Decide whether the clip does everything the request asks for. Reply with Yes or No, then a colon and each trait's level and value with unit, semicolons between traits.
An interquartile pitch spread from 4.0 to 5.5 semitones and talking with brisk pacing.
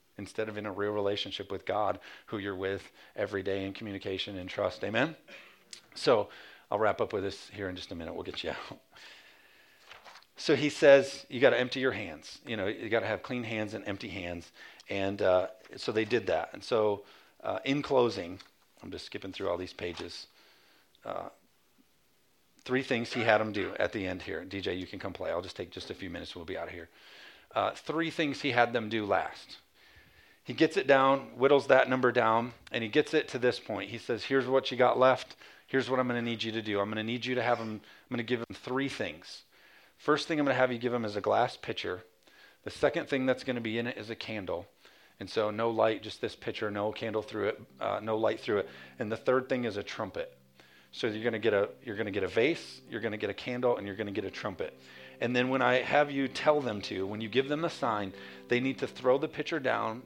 Yes: average, 4.3 semitones; fast, 250 wpm